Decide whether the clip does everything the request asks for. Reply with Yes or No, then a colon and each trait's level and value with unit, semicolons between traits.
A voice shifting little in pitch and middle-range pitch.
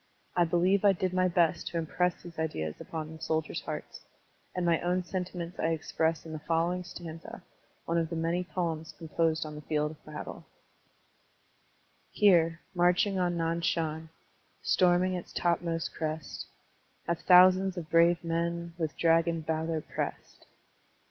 Yes: narrow, 1.8 semitones; medium, 170 Hz